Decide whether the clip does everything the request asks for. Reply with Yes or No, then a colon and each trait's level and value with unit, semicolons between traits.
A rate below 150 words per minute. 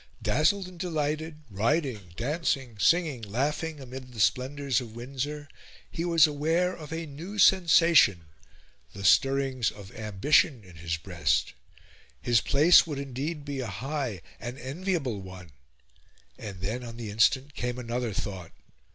Yes: average, 140 wpm